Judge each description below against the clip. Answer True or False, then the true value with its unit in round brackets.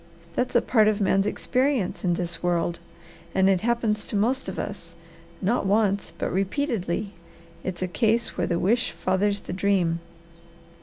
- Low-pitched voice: False (200 Hz)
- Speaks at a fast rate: False (165 wpm)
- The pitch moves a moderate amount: True (3.6 semitones)